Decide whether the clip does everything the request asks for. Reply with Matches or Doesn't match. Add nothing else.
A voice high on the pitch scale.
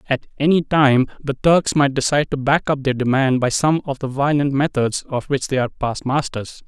Doesn't match